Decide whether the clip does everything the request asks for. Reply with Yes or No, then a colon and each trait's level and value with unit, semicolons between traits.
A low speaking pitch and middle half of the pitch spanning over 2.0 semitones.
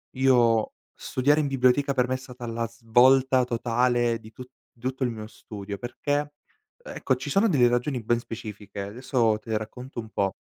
Yes: low, 120 Hz; narrow, 2.5 semitones